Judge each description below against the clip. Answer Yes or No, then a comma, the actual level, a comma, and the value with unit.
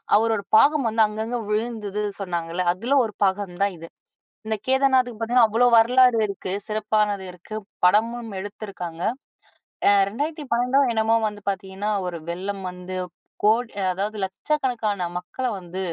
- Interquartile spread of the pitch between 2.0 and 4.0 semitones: Yes, average, 3.6 semitones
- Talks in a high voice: Yes, high, 215 Hz